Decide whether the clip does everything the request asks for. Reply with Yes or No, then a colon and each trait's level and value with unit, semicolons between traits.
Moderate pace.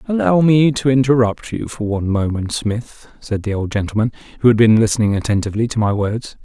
Yes: average, 195 wpm